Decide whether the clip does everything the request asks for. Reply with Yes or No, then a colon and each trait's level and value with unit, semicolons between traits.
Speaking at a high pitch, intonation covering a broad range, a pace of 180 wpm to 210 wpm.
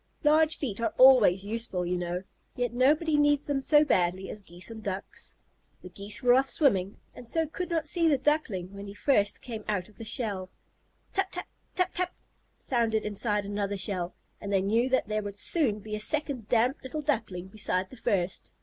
Yes: high, 220 Hz; wide, 6.0 semitones; average, 195 wpm